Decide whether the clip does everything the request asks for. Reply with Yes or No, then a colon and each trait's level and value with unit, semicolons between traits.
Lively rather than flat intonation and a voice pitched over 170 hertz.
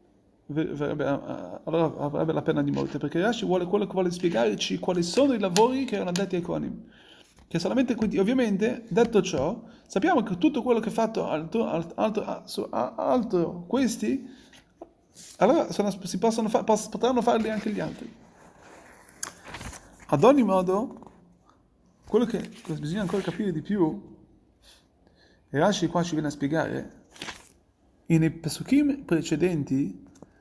Yes: wide, 6.1 semitones; high, 190 Hz